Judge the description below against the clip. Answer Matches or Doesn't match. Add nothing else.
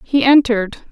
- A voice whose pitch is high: Matches